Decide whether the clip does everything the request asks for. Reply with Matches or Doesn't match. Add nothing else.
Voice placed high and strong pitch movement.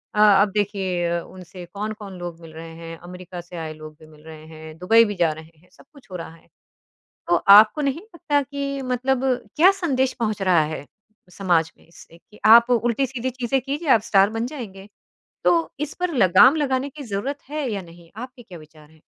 Matches